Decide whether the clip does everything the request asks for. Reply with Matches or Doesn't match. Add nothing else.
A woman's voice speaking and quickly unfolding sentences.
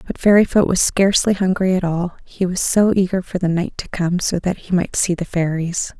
Matches